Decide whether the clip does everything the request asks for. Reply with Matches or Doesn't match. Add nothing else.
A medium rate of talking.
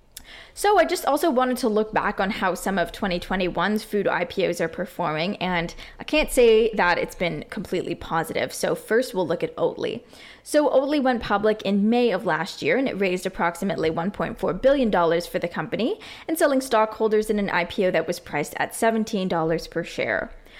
Matches